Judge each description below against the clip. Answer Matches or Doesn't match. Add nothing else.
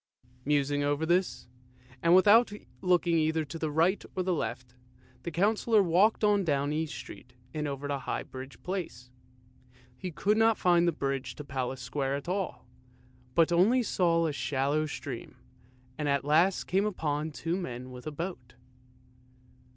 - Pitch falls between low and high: Matches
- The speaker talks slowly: Doesn't match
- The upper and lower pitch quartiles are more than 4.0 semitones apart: Matches